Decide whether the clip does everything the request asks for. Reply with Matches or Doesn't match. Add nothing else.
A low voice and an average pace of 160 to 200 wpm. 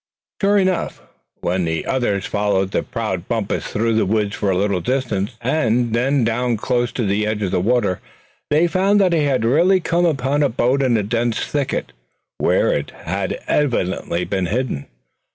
Matches